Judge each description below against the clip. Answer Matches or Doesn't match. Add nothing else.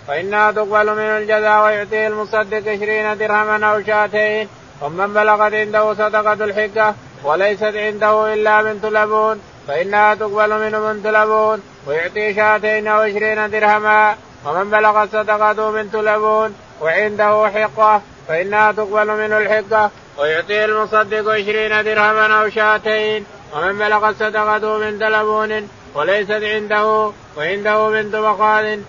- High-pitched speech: Matches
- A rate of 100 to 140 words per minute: Matches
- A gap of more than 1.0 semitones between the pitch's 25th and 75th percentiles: Doesn't match